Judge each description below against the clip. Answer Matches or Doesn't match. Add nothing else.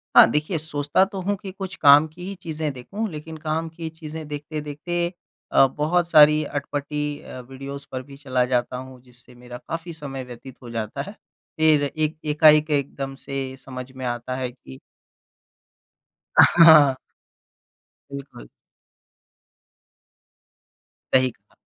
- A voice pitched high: Doesn't match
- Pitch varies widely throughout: Doesn't match